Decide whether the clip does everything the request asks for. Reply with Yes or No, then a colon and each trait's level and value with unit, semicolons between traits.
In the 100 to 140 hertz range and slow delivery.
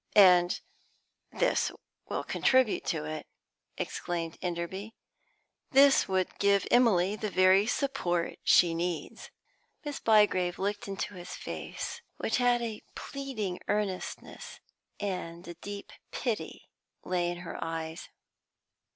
No: high, 190 Hz; slow, 115 wpm